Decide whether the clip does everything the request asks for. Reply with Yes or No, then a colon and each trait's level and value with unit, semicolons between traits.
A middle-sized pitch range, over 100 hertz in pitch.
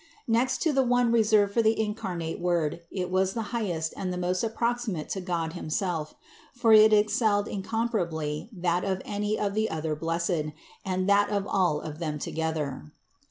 Yes: average, 4.7 semitones; high, 190 Hz